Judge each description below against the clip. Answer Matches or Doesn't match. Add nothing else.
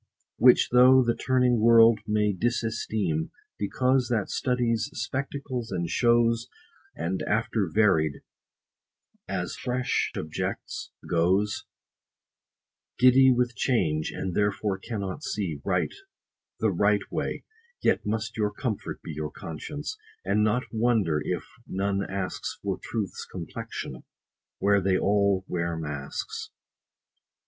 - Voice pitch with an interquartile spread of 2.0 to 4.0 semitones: Doesn't match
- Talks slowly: Matches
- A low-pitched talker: Matches